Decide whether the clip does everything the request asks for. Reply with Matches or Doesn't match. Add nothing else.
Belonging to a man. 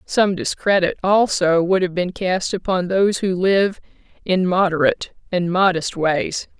Doesn't match